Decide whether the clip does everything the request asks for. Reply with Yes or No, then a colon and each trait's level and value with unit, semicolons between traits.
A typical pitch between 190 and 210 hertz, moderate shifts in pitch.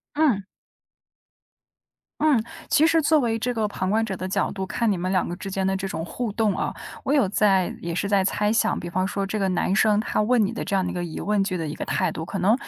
Yes: high, 200 Hz; average, 3.2 semitones